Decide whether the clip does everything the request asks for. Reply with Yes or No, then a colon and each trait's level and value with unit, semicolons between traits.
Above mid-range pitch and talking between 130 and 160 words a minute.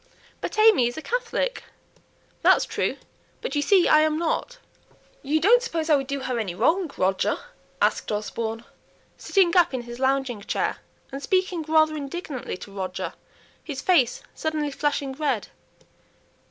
Yes: very high, 290 Hz; average, 155 wpm